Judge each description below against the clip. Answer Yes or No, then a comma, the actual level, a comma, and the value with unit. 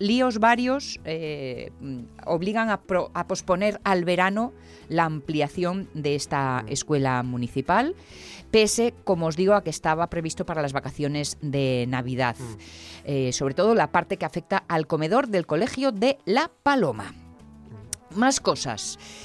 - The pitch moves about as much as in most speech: No, wide, 6.8 semitones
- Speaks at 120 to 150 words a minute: Yes, average, 140 wpm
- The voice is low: No, medium, 160 Hz